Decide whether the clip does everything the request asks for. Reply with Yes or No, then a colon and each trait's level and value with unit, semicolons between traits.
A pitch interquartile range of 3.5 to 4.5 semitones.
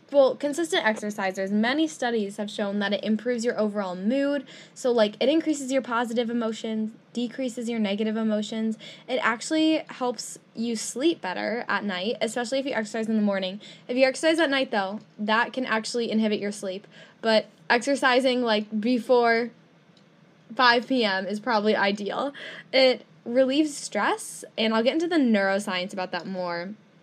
Yes: average, 4.0 semitones